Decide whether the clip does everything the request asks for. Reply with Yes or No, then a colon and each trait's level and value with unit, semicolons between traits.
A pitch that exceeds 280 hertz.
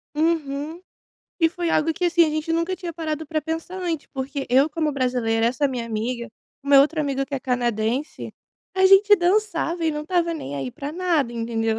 Yes: very high, 300 Hz